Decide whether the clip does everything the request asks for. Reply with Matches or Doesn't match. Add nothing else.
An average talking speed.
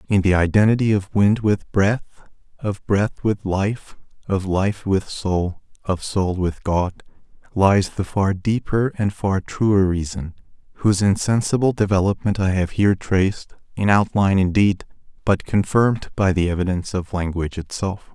Matches